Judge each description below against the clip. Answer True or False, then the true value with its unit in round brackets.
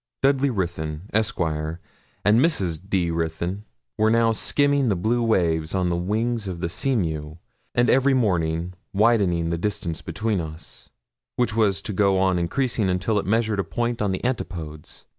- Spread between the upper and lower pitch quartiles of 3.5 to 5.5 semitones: True (5.1 semitones)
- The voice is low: True (95 Hz)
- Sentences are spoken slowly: False (160 wpm)